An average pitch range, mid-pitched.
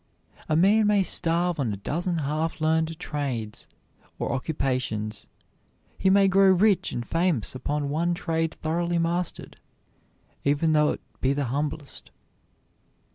Yes: average, 3.7 semitones; medium, 160 Hz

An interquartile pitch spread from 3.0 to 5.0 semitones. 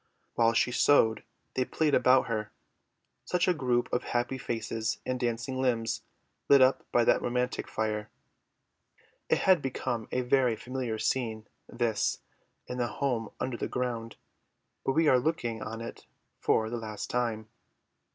No: narrow, 2.4 semitones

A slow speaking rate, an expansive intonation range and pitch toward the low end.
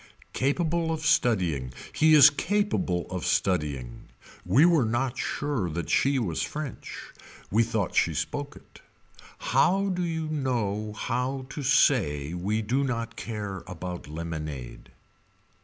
Yes: slow, 130 wpm; wide, 8.4 semitones; low, 115 Hz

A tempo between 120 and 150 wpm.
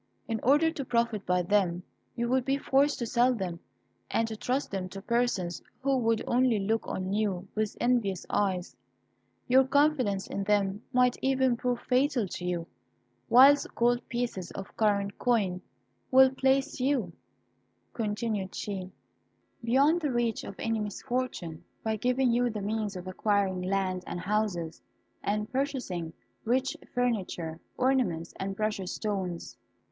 Yes: average, 145 wpm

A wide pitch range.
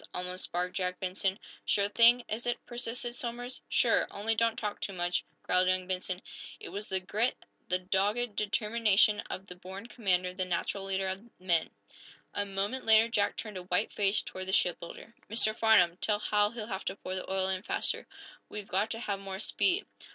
No: average, 3.1 semitones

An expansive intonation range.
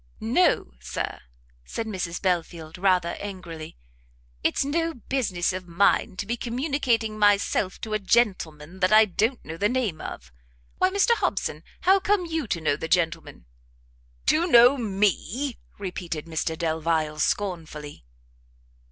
Yes: wide, 6.3 semitones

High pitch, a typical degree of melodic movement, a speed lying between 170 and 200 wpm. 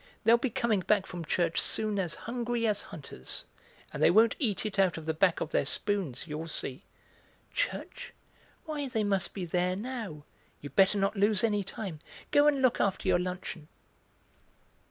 Yes: high, 195 Hz; average, 4.3 semitones; average, 175 wpm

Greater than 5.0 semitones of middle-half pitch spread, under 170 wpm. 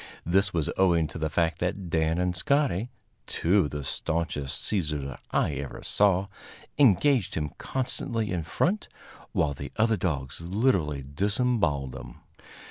Yes: wide, 5.4 semitones; average, 140 wpm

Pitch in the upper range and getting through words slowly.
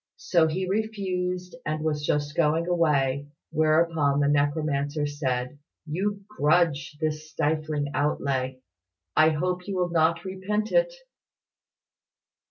No: medium, 155 Hz; slow, 115 wpm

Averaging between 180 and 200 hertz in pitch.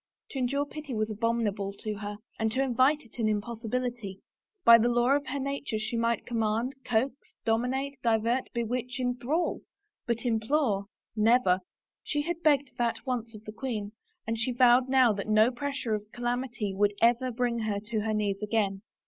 No: high, 235 Hz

